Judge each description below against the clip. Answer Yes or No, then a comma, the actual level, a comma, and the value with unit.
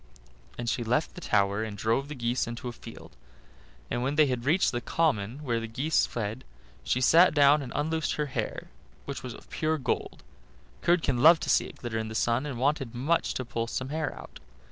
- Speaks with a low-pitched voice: Yes, low, 130 Hz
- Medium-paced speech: No, fast, 210 wpm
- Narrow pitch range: No, average, 4.3 semitones